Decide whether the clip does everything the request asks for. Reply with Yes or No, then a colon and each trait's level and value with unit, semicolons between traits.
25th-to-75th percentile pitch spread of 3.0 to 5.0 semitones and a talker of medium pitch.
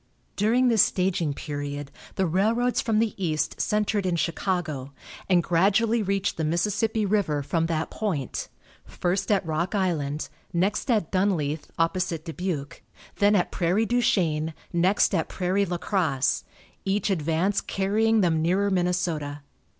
Yes: average, 4.1 semitones; medium, 180 Hz